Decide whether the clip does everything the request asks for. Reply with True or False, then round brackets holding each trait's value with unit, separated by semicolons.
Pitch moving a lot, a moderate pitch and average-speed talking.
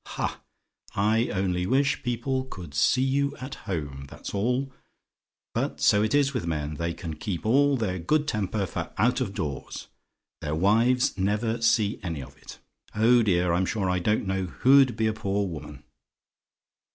False (5.8 semitones; 105 Hz; 170 wpm)